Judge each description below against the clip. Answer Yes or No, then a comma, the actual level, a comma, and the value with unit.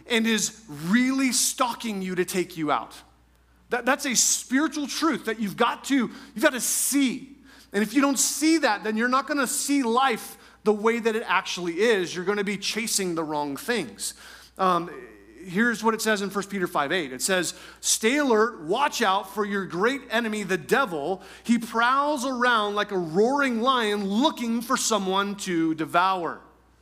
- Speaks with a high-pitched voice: Yes, high, 220 Hz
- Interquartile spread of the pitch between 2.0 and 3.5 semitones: No, average, 5.3 semitones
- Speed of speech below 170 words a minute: No, average, 180 wpm